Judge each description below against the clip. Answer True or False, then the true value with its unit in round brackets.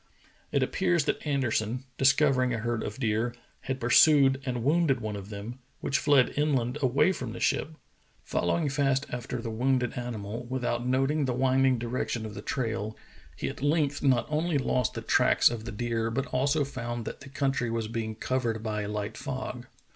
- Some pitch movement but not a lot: True (3.1 semitones)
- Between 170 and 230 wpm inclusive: True (185 wpm)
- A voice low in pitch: True (125 Hz)